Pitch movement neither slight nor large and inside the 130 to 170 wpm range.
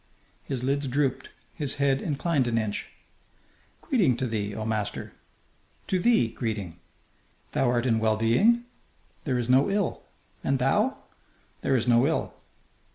Yes: average, 4.3 semitones; average, 145 wpm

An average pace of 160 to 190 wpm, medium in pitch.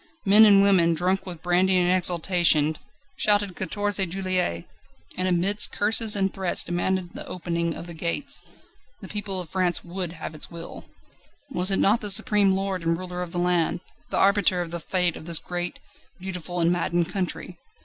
Yes: average, 180 wpm; medium, 180 Hz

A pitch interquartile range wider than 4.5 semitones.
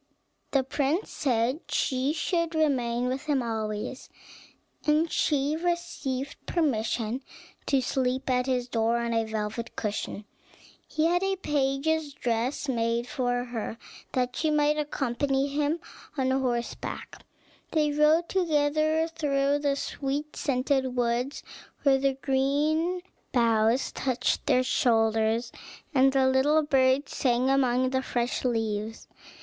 No: average, 3.6 semitones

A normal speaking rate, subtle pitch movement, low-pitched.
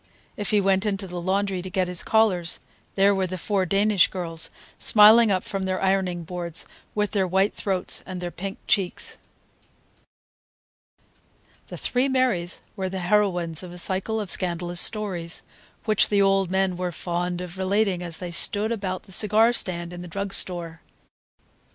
No: average, 170 wpm; narrow, 2.3 semitones; high, 190 Hz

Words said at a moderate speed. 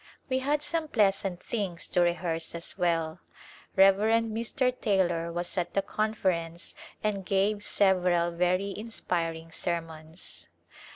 No: slow, 120 wpm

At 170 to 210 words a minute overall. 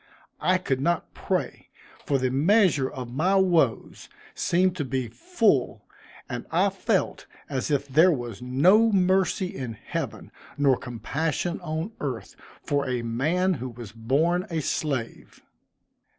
No: slow, 135 wpm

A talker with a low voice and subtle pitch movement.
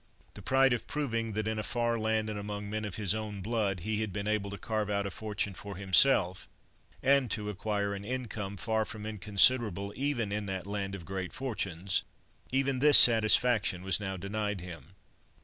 Yes: low, 105 Hz; narrow, 2.3 semitones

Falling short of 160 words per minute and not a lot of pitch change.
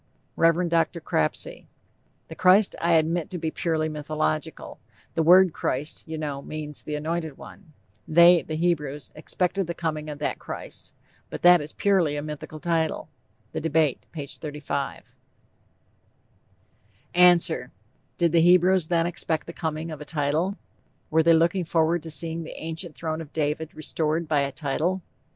Yes: average, 150 wpm; narrow, 2.0 semitones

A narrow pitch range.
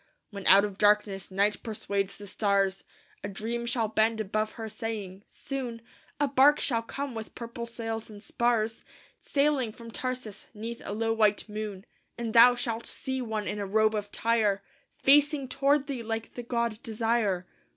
Yes: narrow, 2.3 semitones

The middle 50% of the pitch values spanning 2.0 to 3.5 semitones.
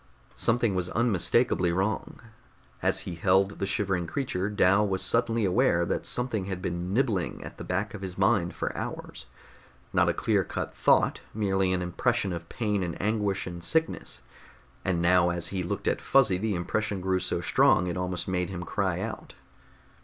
Yes: average, 2.9 semitones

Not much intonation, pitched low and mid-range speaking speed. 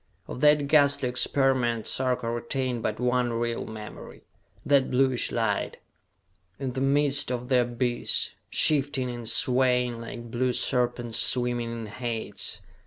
No: narrow, 2.0 semitones; low, 125 Hz; slow, 130 wpm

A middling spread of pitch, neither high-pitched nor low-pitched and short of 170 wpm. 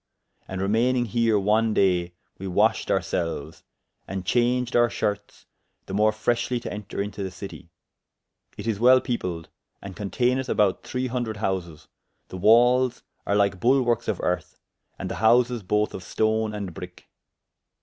No: average, 3.9 semitones; low, 105 Hz; average, 150 wpm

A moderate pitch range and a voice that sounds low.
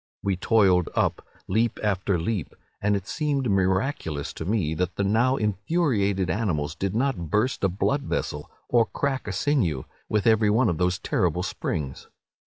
Yes: average, 4.3 semitones; low, 100 Hz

